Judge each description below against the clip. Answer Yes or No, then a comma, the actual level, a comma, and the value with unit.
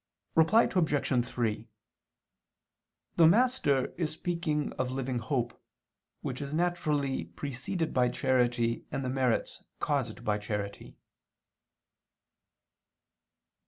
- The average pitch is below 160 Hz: Yes, low, 135 Hz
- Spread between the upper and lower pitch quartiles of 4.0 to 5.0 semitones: Yes, average, 4.7 semitones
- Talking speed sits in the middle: No, slow, 95 wpm